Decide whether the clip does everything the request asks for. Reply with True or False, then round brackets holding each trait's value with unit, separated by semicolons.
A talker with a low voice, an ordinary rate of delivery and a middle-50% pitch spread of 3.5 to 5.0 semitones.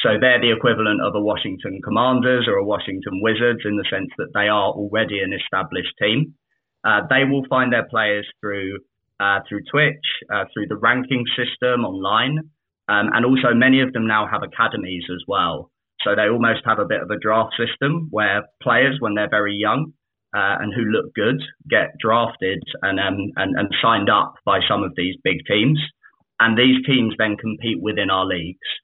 True (115 Hz; 190 wpm; 3.8 semitones)